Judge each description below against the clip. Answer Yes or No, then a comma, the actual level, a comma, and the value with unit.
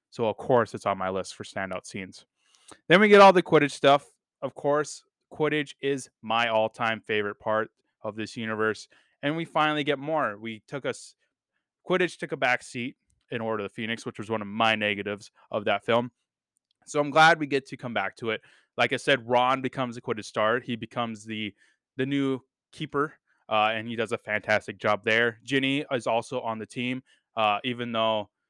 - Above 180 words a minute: Yes, average, 200 wpm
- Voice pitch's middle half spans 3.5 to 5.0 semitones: Yes, average, 4.3 semitones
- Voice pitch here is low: Yes, low, 120 Hz